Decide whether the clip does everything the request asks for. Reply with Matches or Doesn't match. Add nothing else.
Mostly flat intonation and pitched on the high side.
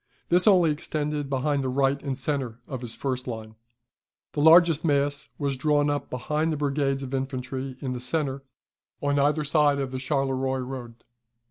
Doesn't match